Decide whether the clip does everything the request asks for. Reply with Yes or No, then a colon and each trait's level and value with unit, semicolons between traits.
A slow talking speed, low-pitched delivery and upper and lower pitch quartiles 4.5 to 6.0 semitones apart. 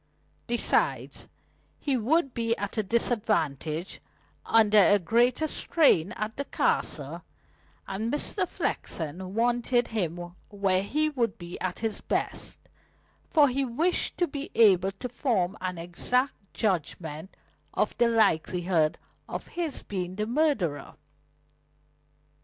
No: slow, 120 wpm; high, 215 Hz; wide, 5.4 semitones